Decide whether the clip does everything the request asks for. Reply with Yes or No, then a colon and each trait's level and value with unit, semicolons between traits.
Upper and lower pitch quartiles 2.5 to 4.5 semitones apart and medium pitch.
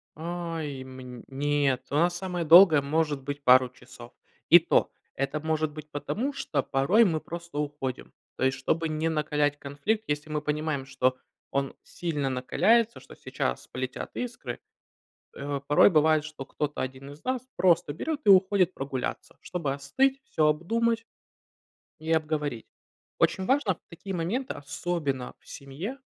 Yes: average, 4.1 semitones; medium, 150 Hz